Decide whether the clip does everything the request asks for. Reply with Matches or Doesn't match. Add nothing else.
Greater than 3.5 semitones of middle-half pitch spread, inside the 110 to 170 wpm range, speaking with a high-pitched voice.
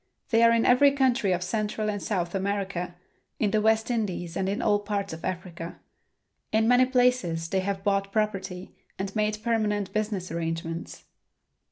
Doesn't match